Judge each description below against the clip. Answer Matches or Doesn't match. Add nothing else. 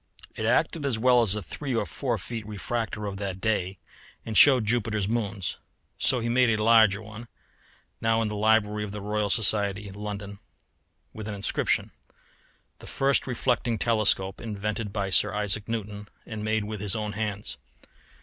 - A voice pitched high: Doesn't match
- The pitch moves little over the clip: Matches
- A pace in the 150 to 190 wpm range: Matches